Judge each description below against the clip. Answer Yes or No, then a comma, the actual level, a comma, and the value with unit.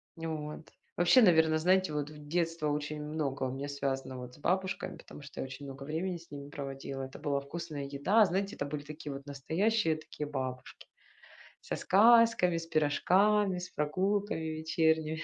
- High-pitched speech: No, medium, 155 Hz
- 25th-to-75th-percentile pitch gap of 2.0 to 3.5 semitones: No, average, 3.9 semitones